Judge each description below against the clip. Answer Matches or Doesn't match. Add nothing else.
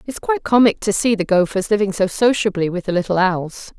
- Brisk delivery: Matches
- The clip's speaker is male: Doesn't match